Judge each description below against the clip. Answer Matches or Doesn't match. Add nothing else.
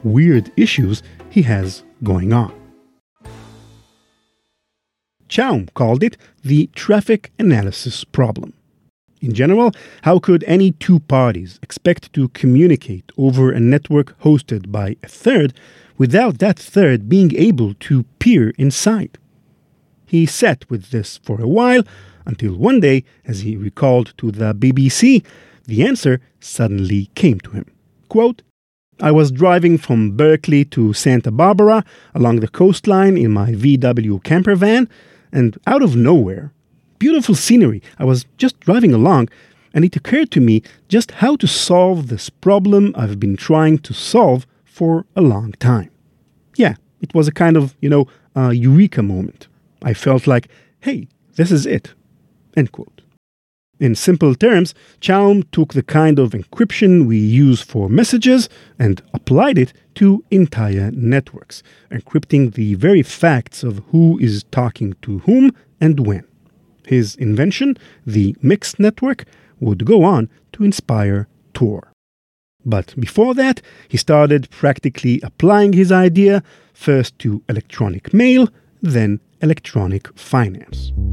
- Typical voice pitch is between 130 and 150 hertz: Matches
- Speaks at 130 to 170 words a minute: Matches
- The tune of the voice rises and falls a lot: Matches